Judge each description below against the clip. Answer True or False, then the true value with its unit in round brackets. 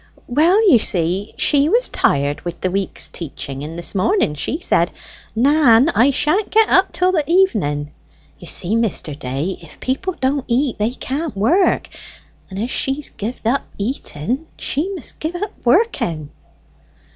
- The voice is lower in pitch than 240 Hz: False (245 Hz)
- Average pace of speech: True (155 wpm)